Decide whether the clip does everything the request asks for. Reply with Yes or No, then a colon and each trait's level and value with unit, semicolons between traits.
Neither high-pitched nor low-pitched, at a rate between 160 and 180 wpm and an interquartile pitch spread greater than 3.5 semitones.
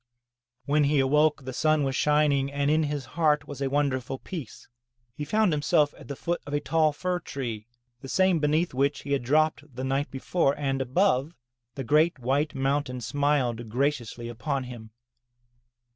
No: medium, 145 Hz; average, 175 wpm; narrow, 2.4 semitones